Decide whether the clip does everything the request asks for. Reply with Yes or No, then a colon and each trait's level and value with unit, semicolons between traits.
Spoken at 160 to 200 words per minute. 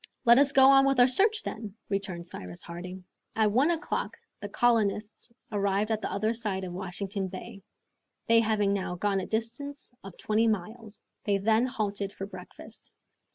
Yes: average, 170 wpm